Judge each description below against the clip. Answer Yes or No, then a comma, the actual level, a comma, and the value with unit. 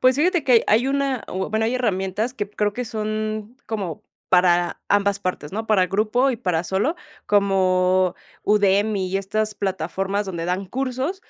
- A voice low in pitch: No, high, 205 Hz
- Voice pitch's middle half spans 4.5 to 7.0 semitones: No, average, 3.4 semitones